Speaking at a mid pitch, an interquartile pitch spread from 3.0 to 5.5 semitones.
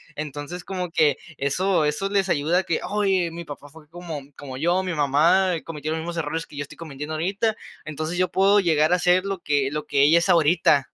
Yes: medium, 165 Hz; average, 3.5 semitones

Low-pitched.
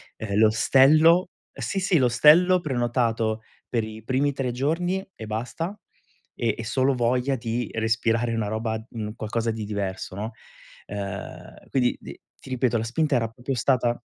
Yes: low, 120 Hz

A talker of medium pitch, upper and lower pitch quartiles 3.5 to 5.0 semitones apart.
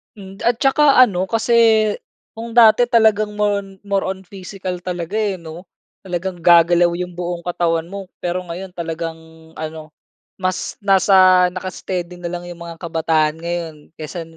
No: medium, 180 Hz; average, 2.8 semitones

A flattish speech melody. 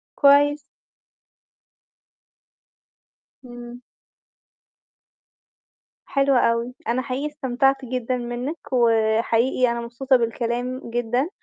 Yes: narrow, 2.2 semitones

